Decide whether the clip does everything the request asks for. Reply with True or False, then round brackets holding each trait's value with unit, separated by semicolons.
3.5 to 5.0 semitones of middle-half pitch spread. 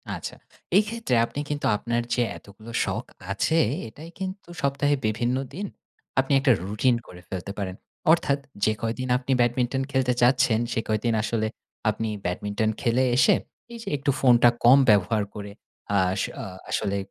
True (4.2 semitones)